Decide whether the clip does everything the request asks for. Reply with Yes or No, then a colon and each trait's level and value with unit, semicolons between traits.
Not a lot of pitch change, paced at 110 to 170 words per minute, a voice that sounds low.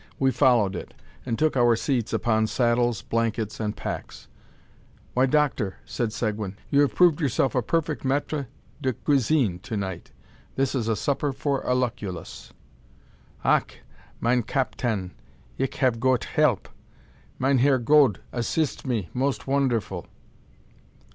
No: average, 3.9 semitones; slow, 135 wpm; low, 125 Hz